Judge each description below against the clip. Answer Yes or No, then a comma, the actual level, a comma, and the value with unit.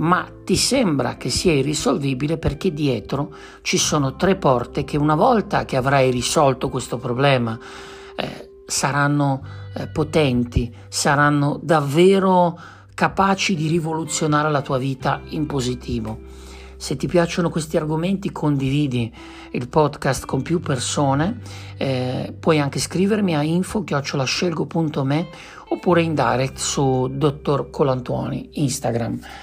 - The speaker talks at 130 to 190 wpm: No, average, 120 wpm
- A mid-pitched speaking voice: Yes, medium, 145 Hz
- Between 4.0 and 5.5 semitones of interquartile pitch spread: Yes, average, 4.3 semitones